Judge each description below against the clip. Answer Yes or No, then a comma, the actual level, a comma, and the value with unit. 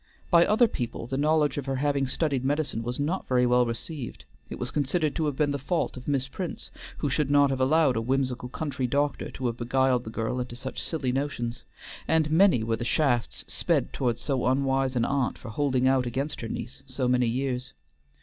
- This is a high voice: No, low, 135 Hz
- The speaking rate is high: Yes, fast, 210 wpm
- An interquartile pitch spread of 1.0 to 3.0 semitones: Yes, average, 2.7 semitones